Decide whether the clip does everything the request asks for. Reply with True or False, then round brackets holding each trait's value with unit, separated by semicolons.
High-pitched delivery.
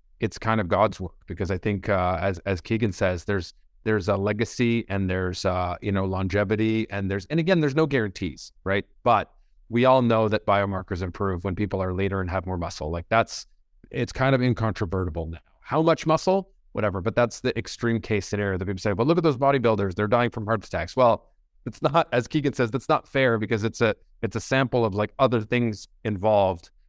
False (105 Hz)